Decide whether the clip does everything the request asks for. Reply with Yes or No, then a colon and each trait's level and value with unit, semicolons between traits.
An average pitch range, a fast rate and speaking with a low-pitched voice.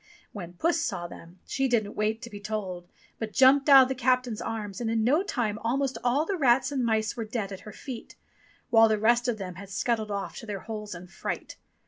No: average, 3.6 semitones; fast, 225 wpm; high, 225 Hz